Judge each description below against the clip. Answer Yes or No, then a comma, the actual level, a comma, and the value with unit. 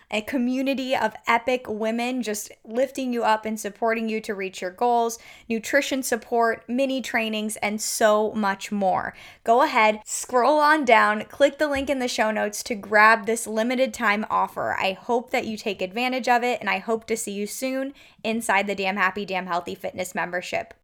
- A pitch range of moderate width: Yes, average, 3.0 semitones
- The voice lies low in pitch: No, high, 225 Hz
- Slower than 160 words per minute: No, average, 185 wpm